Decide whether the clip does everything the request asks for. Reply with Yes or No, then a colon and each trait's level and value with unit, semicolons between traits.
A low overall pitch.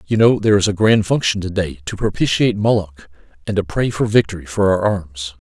Yes: low, 100 Hz